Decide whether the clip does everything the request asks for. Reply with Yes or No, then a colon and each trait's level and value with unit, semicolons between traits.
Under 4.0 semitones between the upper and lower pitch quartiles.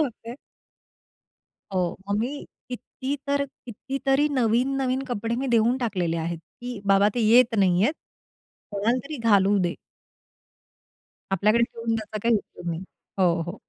No: average, 4.4 semitones